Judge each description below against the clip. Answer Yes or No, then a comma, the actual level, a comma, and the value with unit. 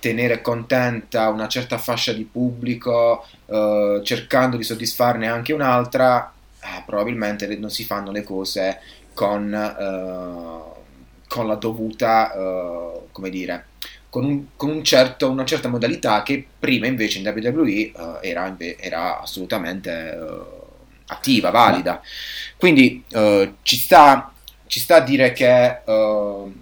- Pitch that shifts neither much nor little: Yes, average, 3.7 semitones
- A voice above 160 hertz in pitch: No, low, 115 Hz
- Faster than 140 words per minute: No, slow, 115 wpm